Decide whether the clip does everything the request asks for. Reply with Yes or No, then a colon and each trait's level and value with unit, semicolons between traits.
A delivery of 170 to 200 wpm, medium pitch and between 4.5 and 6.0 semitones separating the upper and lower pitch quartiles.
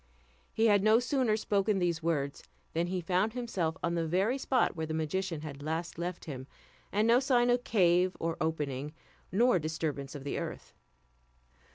Yes: average, 175 wpm; medium, 175 Hz; average, 5.2 semitones